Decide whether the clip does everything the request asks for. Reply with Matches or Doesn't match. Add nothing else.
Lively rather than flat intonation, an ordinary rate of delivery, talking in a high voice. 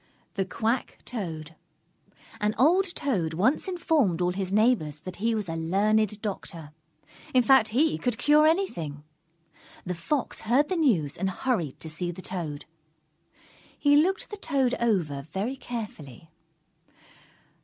Matches